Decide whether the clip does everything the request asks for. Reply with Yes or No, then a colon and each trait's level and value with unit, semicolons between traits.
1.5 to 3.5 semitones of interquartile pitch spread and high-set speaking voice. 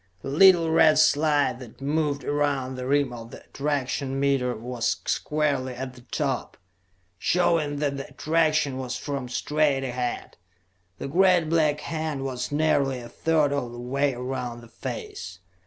No: average, 3.2 semitones; medium, 140 Hz